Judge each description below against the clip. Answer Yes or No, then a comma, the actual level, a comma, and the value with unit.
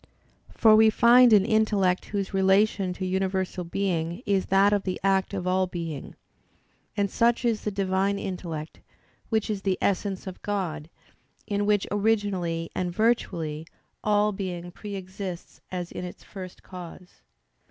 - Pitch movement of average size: No, narrow, 2.2 semitones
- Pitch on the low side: No, high, 190 Hz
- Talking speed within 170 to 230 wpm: No, average, 150 wpm